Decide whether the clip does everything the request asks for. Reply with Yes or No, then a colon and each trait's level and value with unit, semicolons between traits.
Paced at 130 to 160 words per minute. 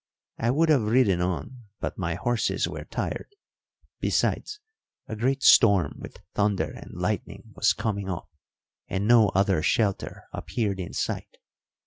Yes: average, 140 wpm